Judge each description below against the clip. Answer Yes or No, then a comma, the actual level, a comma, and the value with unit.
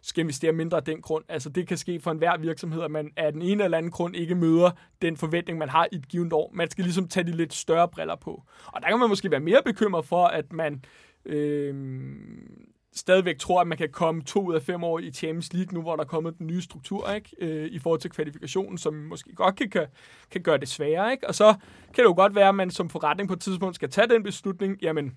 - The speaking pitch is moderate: Yes, medium, 170 Hz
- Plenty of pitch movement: No, average, 3.0 semitones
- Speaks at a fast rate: Yes, fast, 255 wpm